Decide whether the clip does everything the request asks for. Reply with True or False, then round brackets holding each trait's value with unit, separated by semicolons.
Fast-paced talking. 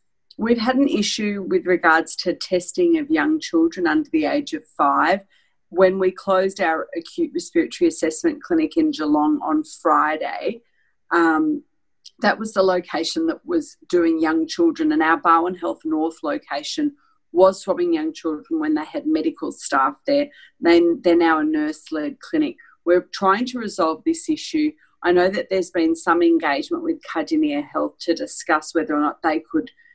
False (170 wpm)